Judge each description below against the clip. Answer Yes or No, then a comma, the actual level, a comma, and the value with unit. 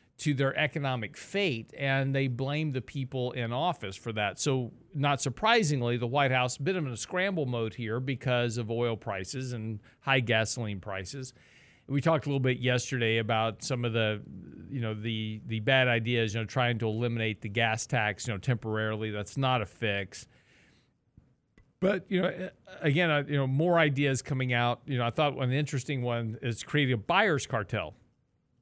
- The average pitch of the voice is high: No, low, 125 Hz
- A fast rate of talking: No, average, 185 wpm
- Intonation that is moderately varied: Yes, average, 3.7 semitones